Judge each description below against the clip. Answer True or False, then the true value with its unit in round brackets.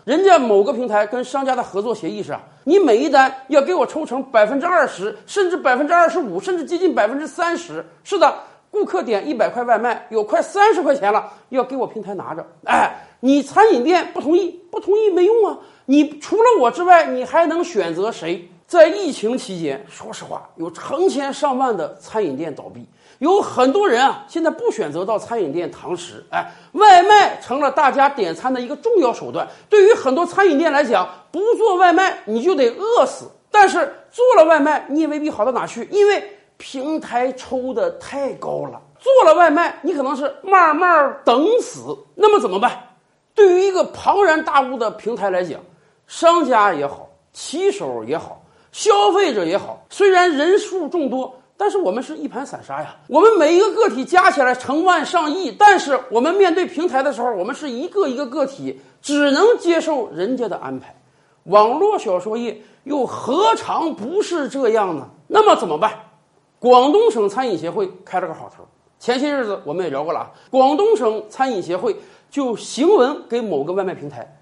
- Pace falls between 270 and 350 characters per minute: True (280 characters per minute)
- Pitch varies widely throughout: True (7.4 semitones)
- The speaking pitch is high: True (305 Hz)